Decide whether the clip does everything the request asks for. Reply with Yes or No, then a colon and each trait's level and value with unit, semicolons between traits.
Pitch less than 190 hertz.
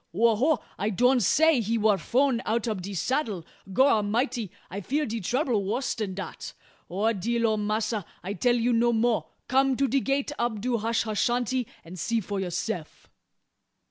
No: high, 230 Hz